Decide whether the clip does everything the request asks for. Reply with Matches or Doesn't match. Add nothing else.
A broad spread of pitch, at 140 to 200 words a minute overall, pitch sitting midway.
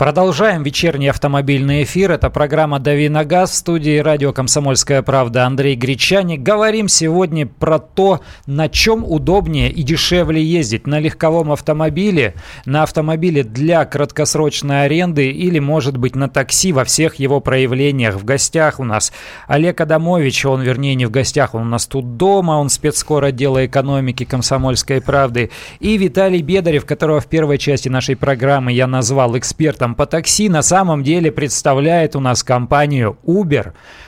Doesn't match